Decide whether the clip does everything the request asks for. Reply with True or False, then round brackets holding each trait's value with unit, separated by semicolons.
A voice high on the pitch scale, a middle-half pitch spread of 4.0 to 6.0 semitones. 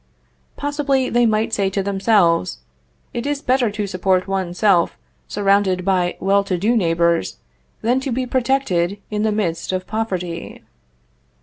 True (200 Hz; 4.3 semitones)